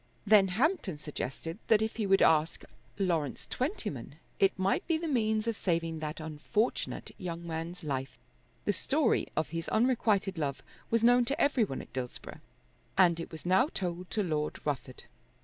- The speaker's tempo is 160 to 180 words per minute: Yes, average, 165 wpm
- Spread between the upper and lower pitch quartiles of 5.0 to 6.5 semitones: Yes, wide, 5.6 semitones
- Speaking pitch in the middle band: Yes, medium, 180 Hz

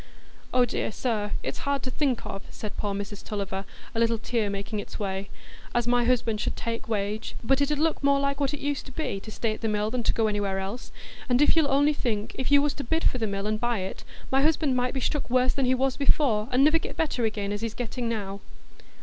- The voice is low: No, high, 240 Hz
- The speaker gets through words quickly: Yes, fast, 245 wpm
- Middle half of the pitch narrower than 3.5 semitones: No, average, 4.6 semitones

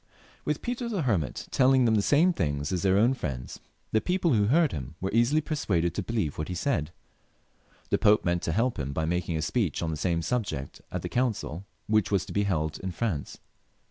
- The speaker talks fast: Yes, fast, 215 wpm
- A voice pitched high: No, low, 100 Hz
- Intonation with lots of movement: Yes, wide, 7.5 semitones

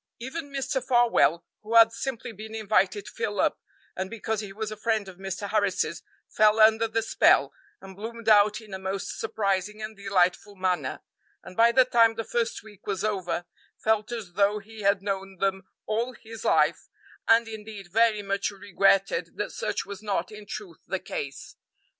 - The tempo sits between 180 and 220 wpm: Yes, average, 185 wpm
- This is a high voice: Yes, high, 210 Hz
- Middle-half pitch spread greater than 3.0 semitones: No, narrow, 2.4 semitones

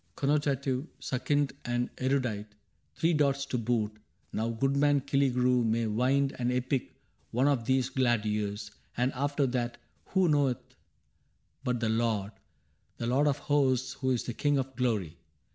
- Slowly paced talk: No, average, 155 wpm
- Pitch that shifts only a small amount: No, average, 3.0 semitones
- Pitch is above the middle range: No, low, 125 Hz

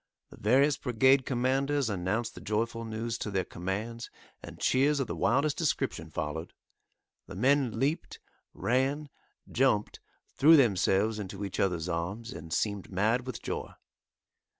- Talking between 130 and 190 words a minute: Yes, average, 140 wpm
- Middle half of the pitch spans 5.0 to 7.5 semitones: Yes, wide, 5.4 semitones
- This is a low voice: Yes, low, 115 Hz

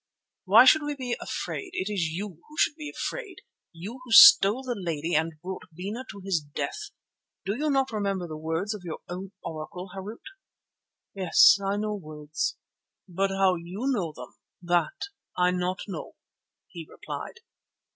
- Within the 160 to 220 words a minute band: Yes, average, 165 wpm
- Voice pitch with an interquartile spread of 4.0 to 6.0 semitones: Yes, average, 4.6 semitones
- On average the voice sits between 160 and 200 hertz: Yes, high, 190 Hz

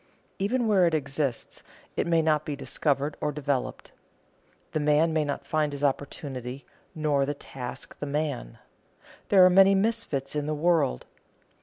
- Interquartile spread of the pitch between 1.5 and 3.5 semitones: Yes, average, 2.8 semitones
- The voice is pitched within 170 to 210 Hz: No, medium, 150 Hz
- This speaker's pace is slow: No, average, 155 wpm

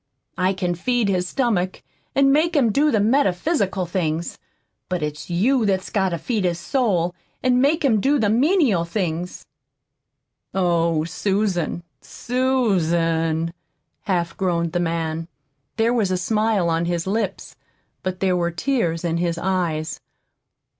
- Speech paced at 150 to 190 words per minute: No, average, 140 wpm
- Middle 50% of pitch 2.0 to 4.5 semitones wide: No, average, 5.1 semitones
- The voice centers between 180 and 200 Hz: Yes, medium, 185 Hz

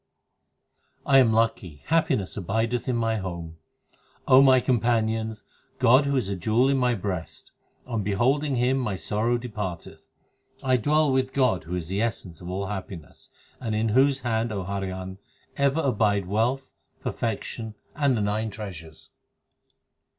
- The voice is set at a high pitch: No, low, 110 Hz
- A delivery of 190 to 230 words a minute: No, average, 160 wpm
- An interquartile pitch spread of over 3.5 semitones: Yes, average, 4.6 semitones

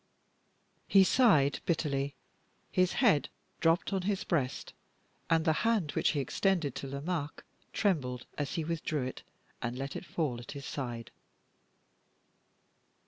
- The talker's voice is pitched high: No, medium, 150 Hz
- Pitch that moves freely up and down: No, average, 4.8 semitones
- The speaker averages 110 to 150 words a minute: Yes, average, 140 wpm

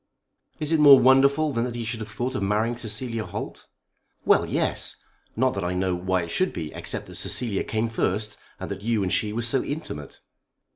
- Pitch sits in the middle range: No, low, 115 Hz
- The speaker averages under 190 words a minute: No, fast, 205 wpm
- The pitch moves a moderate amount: Yes, average, 4.6 semitones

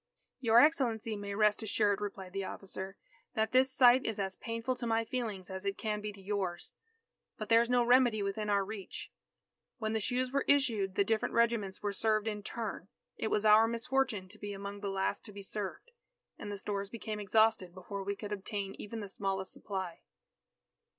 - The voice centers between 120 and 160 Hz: No, high, 210 Hz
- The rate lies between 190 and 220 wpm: Yes, average, 195 wpm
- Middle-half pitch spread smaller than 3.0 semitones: Yes, narrow, 2.5 semitones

